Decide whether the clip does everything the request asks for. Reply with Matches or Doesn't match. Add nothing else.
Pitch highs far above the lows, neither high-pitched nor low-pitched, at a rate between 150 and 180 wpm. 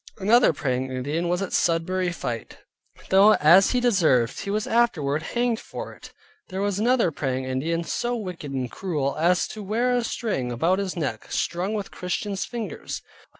Matches